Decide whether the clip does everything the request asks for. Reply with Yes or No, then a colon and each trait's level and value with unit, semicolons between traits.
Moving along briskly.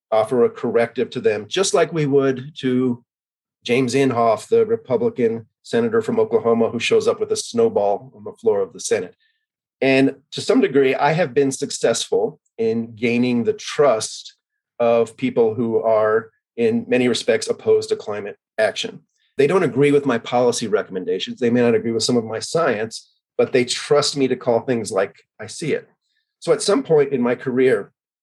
No: average, 185 wpm